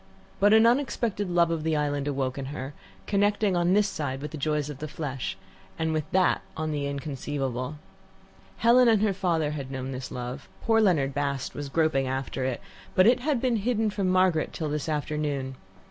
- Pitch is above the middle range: No, medium, 155 Hz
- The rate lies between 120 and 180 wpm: No, average, 190 wpm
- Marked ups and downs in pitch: Yes, wide, 6.1 semitones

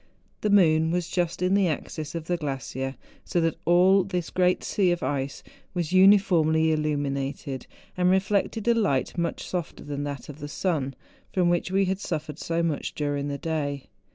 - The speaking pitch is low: No, medium, 165 Hz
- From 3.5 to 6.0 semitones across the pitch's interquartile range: Yes, average, 4.0 semitones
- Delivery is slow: No, average, 180 wpm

